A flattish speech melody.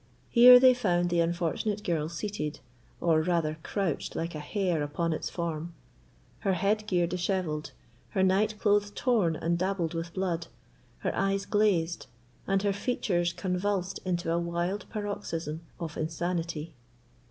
No: average, 3.2 semitones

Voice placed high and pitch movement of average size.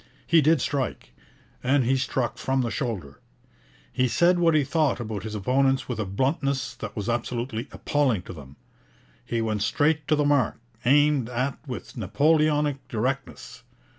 No: low, 130 Hz; average, 4.2 semitones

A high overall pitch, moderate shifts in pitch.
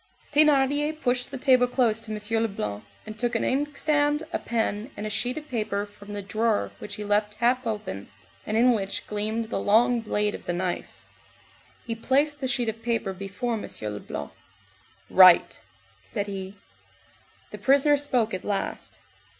Yes: high, 225 Hz; average, 3.7 semitones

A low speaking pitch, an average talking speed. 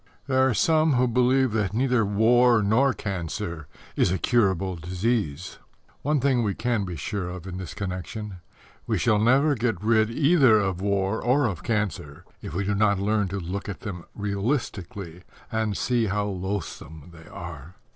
Yes: low, 105 Hz; average, 170 wpm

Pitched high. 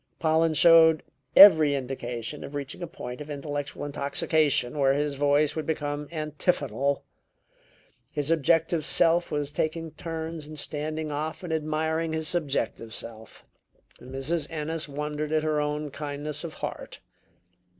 No: medium, 150 Hz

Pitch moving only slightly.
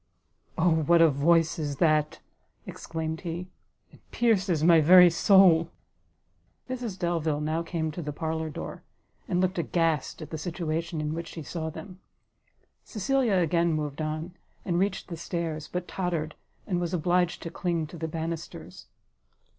Yes: narrow, 2.1 semitones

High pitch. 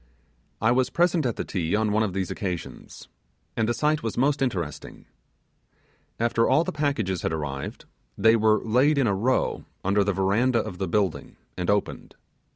No: low, 110 Hz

